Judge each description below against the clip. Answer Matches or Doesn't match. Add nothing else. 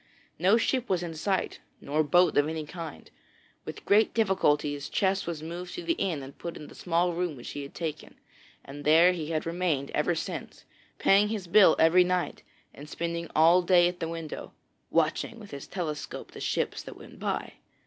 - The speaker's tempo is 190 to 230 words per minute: Matches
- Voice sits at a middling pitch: Matches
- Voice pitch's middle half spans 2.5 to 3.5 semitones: Matches